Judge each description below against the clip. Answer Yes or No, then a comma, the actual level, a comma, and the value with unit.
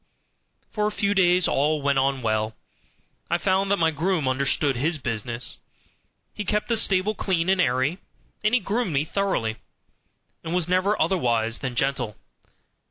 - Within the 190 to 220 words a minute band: No, average, 160 wpm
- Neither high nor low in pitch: Yes, medium, 160 Hz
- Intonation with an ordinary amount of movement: No, wide, 6.8 semitones